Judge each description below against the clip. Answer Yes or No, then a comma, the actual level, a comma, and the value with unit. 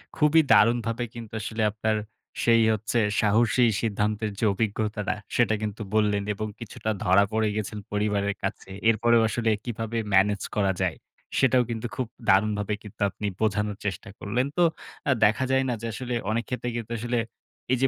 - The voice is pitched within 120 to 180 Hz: No, low, 110 Hz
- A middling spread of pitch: No, narrow, 2.2 semitones